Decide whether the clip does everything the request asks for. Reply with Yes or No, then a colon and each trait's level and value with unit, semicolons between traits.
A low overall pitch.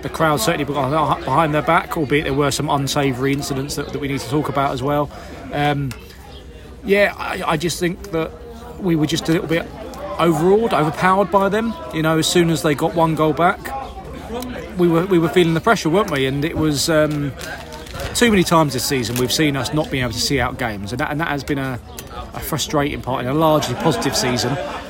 No: medium, 150 Hz